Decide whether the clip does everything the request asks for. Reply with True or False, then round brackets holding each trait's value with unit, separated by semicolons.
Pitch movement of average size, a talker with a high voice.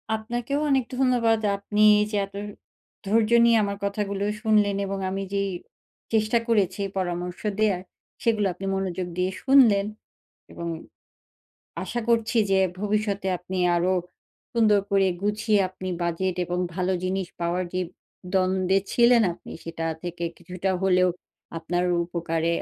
True (3.0 semitones; 195 Hz)